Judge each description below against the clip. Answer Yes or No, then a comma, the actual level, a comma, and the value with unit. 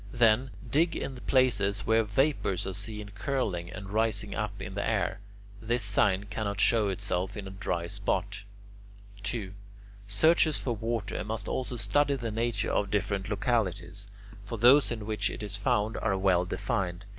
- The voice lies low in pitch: Yes, low, 105 Hz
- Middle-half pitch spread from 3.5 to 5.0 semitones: No, average, 3.0 semitones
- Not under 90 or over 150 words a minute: No, average, 160 wpm